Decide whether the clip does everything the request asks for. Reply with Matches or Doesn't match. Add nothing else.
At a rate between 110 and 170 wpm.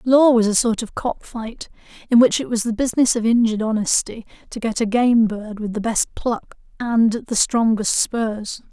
Doesn't match